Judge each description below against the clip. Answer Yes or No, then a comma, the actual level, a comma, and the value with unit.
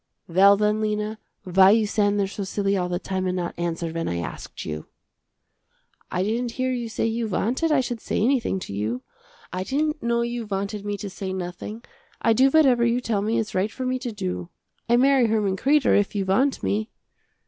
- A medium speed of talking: No, fast, 210 wpm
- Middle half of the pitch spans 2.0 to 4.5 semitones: Yes, average, 3.9 semitones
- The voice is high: Yes, high, 210 Hz